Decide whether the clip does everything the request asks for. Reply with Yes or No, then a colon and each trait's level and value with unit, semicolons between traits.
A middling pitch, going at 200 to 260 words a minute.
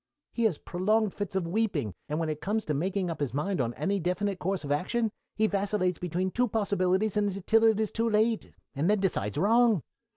No: high, 195 Hz; fast, 205 wpm